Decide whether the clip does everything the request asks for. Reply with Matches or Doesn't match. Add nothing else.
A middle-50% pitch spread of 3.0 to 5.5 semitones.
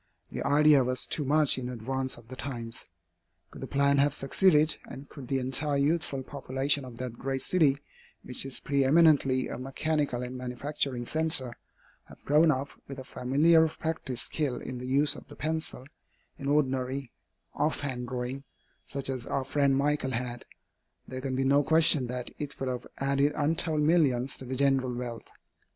Doesn't match